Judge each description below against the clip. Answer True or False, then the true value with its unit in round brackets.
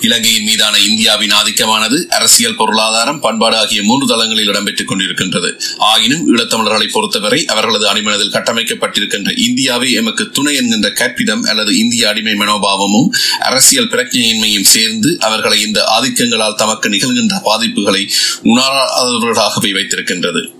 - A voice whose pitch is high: True (225 Hz)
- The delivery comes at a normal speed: True (110 wpm)